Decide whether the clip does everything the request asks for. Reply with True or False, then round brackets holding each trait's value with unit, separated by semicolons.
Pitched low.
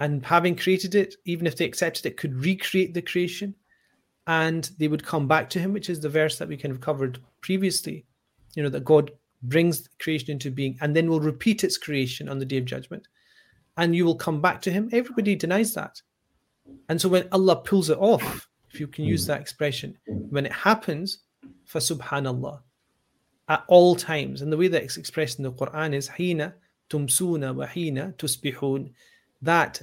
False (160 Hz)